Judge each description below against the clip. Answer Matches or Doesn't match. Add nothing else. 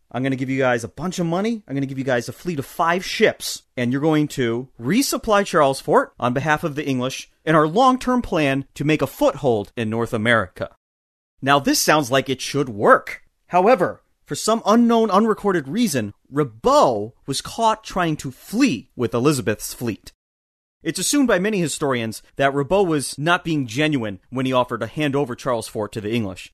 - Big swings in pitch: Matches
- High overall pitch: Doesn't match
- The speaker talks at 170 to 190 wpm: Doesn't match